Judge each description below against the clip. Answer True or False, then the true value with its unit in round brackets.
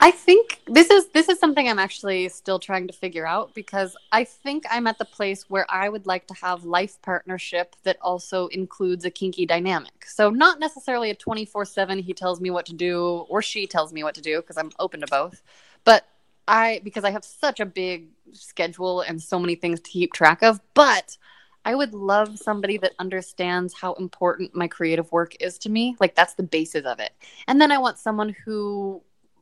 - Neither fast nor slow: False (210 wpm)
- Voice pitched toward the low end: False (190 Hz)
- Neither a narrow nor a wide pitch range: True (3.6 semitones)